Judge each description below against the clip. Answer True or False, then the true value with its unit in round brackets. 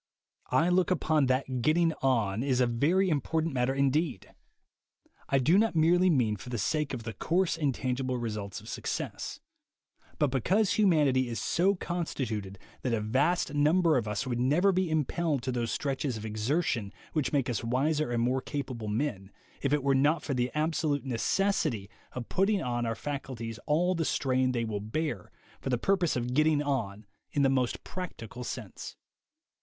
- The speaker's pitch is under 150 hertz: True (135 Hz)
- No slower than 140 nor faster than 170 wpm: False (180 wpm)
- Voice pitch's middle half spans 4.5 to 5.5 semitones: True (4.9 semitones)